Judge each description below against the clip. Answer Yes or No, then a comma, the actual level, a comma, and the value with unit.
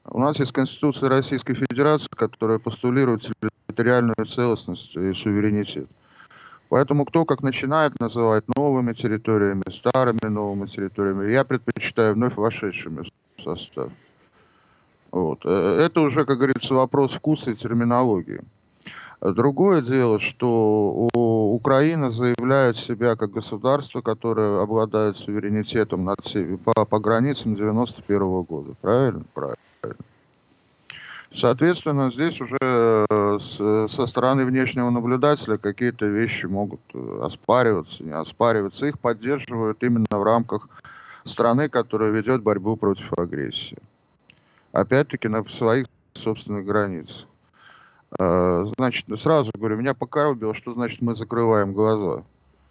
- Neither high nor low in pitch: No, low, 115 Hz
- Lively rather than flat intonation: No, average, 3.5 semitones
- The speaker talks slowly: Yes, slow, 105 wpm